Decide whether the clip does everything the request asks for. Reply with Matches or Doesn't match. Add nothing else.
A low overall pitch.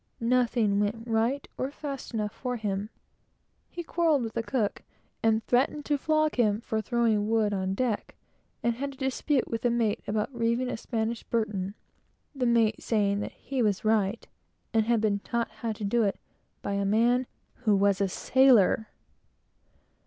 Doesn't match